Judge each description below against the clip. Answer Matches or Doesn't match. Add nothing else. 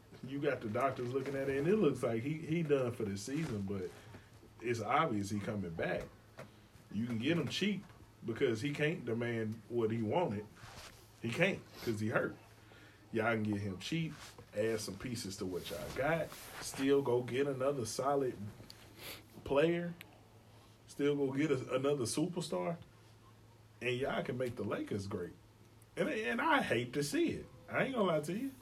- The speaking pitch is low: Matches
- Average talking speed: Matches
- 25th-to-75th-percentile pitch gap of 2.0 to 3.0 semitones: Doesn't match